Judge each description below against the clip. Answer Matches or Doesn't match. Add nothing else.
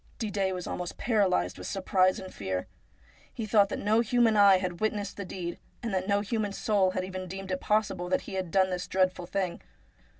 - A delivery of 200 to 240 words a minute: Matches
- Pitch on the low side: Doesn't match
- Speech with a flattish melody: Matches